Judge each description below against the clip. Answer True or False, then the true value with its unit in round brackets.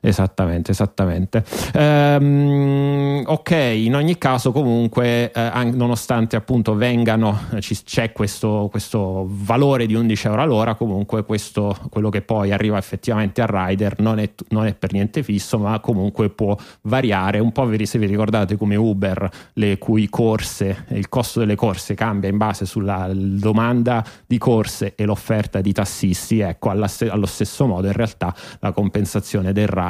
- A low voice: True (110 Hz)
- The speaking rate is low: False (155 wpm)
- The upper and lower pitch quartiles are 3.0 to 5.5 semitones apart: False (2.6 semitones)